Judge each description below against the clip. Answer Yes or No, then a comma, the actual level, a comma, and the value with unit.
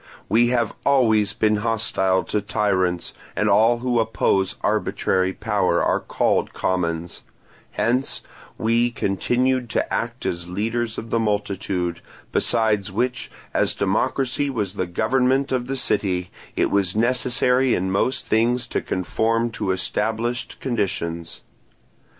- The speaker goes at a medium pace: No, slow, 125 wpm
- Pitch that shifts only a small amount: No, average, 4.1 semitones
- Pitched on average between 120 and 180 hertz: No, low, 110 Hz